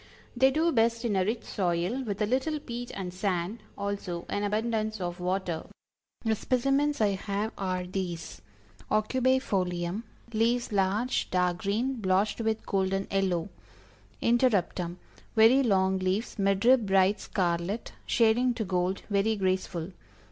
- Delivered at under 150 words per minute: Yes, average, 140 wpm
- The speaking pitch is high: Yes, high, 200 Hz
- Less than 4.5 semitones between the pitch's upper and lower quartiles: Yes, average, 3.8 semitones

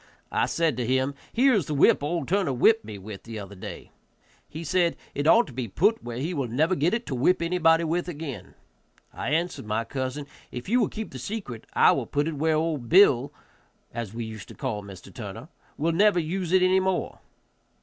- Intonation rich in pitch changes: Yes, wide, 6.6 semitones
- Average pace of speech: No, fast, 215 wpm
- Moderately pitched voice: Yes, medium, 155 Hz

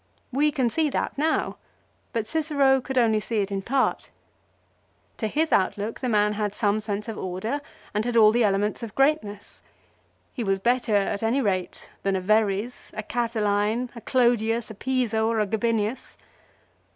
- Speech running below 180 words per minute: Yes, average, 170 wpm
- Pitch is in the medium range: No, high, 225 Hz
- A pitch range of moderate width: Yes, average, 3.2 semitones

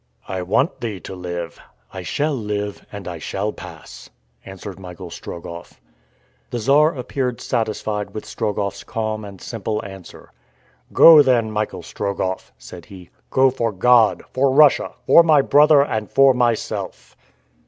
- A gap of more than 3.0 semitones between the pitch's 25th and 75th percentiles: Yes, average, 5.3 semitones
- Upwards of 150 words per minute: No, average, 145 wpm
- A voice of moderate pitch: No, low, 110 Hz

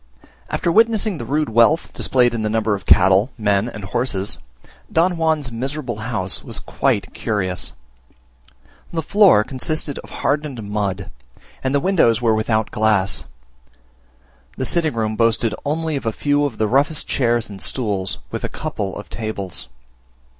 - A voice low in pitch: Yes, low, 115 Hz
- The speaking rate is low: No, average, 155 wpm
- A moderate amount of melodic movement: No, wide, 5.7 semitones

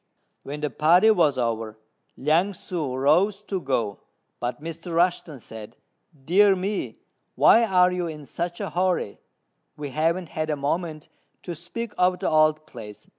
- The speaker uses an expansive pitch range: No, average, 4.2 semitones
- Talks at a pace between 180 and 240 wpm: No, average, 155 wpm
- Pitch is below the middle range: No, medium, 160 Hz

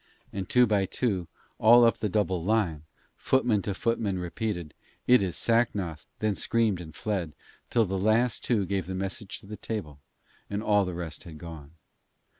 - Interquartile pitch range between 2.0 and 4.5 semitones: Yes, average, 3.9 semitones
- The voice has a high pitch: No, low, 100 Hz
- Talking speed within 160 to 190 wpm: Yes, average, 175 wpm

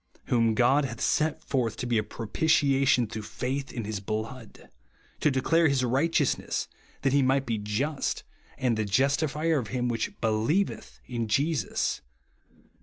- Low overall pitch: Yes, low, 125 Hz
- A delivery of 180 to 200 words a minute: No, average, 155 wpm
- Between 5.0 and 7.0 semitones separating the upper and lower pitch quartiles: No, average, 4.0 semitones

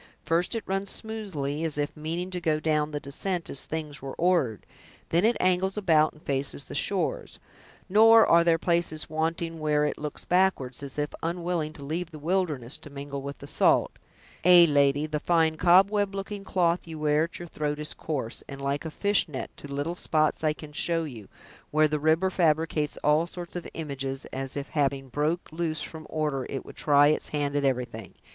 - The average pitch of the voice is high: No, medium, 155 Hz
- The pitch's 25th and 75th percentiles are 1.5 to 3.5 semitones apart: Yes, average, 3.1 semitones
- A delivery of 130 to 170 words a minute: No, average, 195 wpm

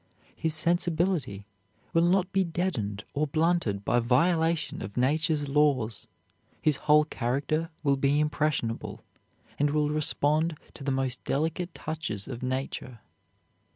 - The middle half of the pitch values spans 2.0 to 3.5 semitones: No, average, 3.9 semitones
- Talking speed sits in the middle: No, slow, 125 wpm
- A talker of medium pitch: Yes, medium, 150 Hz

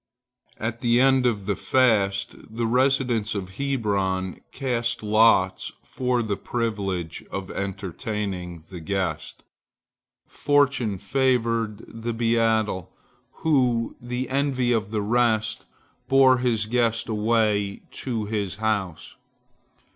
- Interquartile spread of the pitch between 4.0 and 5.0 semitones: No, average, 3.4 semitones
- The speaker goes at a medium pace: No, slow, 110 wpm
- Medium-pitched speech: No, low, 110 Hz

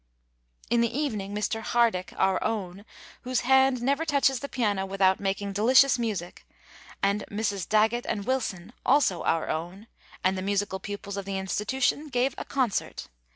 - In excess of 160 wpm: No, average, 155 wpm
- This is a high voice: Yes, high, 210 Hz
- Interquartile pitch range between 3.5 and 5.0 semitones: Yes, average, 4.5 semitones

